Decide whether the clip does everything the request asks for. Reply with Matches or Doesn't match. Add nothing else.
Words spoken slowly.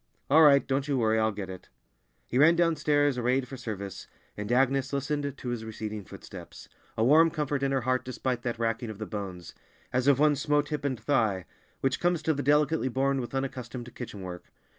Doesn't match